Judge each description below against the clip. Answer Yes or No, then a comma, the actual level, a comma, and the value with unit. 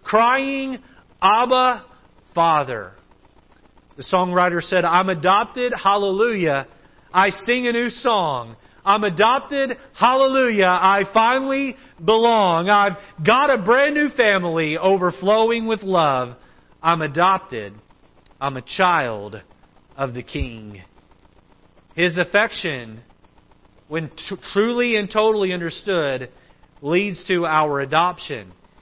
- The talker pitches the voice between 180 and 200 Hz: Yes, high, 190 Hz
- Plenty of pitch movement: Yes, wide, 6.4 semitones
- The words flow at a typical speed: No, slow, 100 wpm